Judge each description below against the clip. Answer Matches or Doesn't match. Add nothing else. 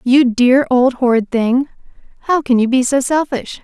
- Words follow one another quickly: Doesn't match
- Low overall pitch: Doesn't match